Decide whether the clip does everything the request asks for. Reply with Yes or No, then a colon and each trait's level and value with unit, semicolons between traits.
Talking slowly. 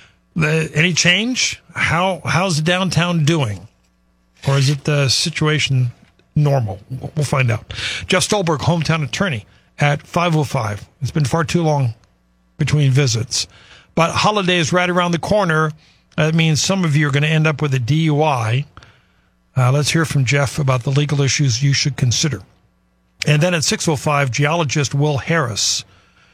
No: average, 155 wpm